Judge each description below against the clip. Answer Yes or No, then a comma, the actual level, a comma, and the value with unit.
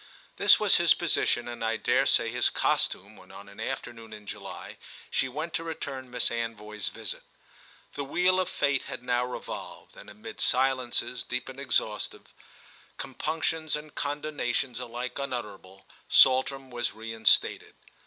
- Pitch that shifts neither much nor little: Yes, average, 3.6 semitones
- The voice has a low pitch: Yes, low, 125 Hz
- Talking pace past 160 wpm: No, average, 145 wpm